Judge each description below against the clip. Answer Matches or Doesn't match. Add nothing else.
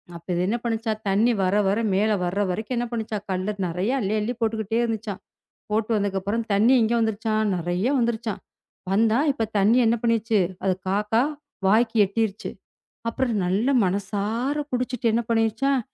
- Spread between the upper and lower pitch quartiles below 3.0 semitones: Matches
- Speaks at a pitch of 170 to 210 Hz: Doesn't match